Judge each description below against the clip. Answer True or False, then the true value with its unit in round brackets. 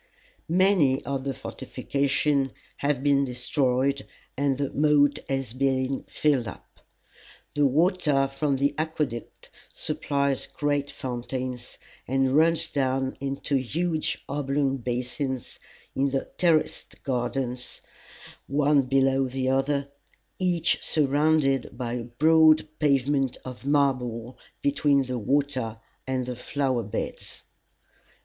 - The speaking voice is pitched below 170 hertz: True (135 Hz)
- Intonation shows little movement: True (2.0 semitones)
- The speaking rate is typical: False (110 wpm)